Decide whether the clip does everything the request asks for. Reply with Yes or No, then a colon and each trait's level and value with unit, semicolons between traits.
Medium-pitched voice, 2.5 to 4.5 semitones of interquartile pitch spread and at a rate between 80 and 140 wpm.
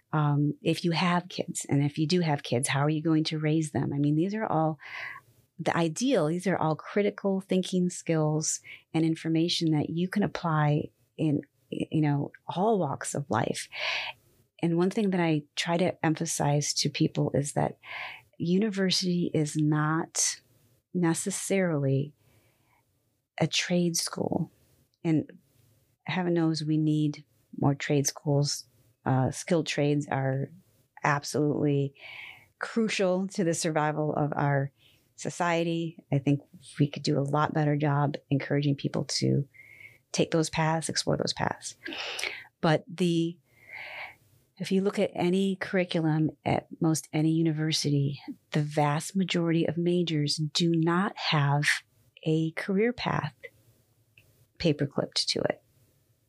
Yes: medium, 155 Hz; average, 3.1 semitones; slow, 135 wpm